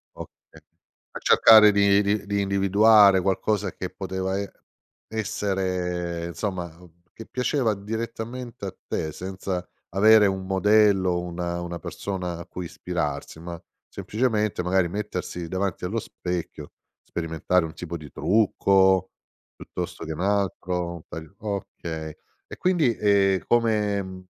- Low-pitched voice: Yes, very low, 95 Hz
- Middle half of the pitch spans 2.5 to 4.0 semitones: Yes, average, 2.8 semitones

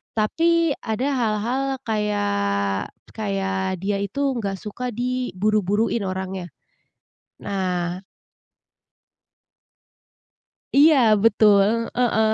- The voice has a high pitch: Yes, high, 210 Hz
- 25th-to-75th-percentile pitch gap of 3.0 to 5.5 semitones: Yes, average, 3.7 semitones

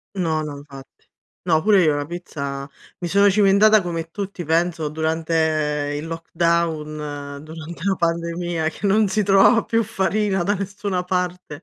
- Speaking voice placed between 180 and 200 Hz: No, medium, 170 Hz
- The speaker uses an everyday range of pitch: Yes, average, 3.7 semitones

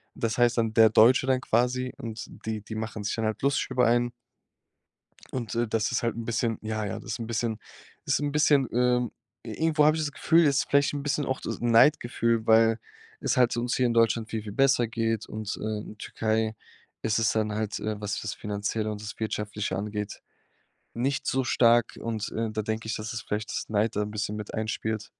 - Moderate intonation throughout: No, narrow, 2.2 semitones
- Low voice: Yes, low, 115 Hz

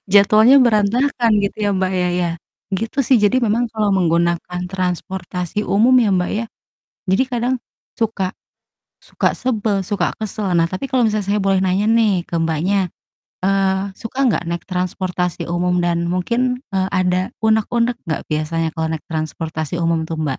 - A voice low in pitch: No, high, 190 Hz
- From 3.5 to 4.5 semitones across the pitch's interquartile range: Yes, average, 3.8 semitones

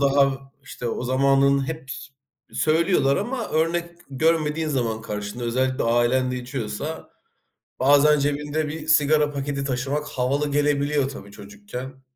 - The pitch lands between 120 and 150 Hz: Yes, medium, 140 Hz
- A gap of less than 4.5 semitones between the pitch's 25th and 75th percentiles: Yes, average, 2.7 semitones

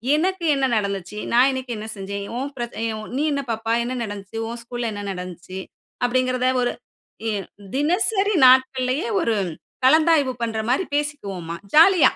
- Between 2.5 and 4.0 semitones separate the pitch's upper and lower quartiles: No, average, 5.2 semitones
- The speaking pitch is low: No, very high, 255 Hz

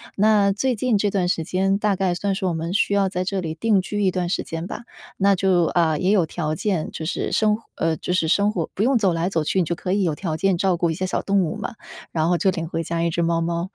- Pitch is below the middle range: No, medium, 185 Hz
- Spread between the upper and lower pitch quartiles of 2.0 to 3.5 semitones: Yes, average, 3.1 semitones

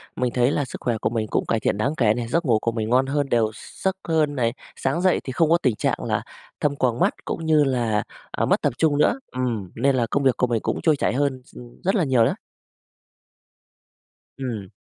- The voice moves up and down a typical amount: Yes, average, 3.9 semitones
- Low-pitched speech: Yes, low, 130 Hz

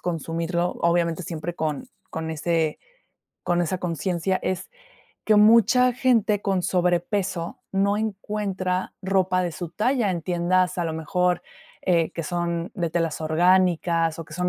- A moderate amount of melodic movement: No, narrow, 2.3 semitones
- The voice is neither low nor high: Yes, medium, 180 Hz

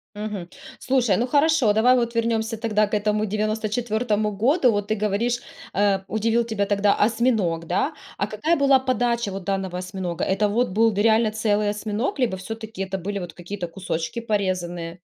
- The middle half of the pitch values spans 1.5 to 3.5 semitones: Yes, average, 3.0 semitones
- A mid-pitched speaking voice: No, high, 215 Hz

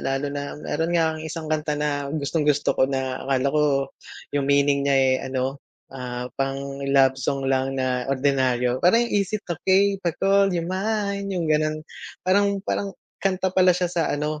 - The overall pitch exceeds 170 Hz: No, medium, 145 Hz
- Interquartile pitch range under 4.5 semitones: No, average, 5.0 semitones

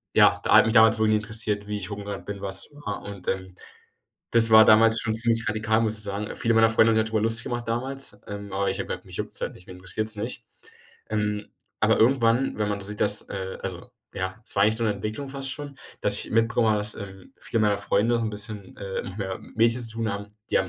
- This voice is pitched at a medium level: No, low, 110 Hz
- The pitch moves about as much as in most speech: No, narrow, 1.9 semitones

